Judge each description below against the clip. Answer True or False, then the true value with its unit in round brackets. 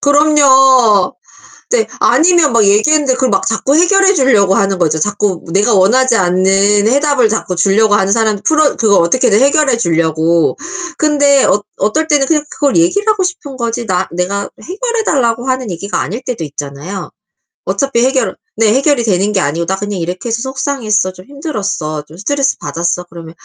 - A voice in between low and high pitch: False (225 Hz)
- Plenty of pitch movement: True (6.7 semitones)